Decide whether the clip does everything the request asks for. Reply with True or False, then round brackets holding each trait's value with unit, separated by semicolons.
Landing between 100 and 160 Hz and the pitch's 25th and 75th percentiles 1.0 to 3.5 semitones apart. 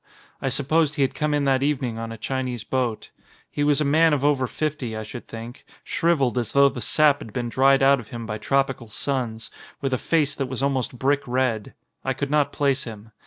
True (135 Hz; 3.1 semitones)